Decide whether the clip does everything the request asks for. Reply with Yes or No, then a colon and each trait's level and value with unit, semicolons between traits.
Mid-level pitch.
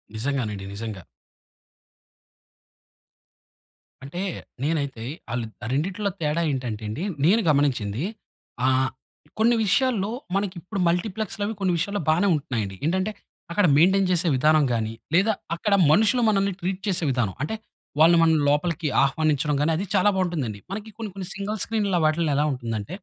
Yes: medium, 165 Hz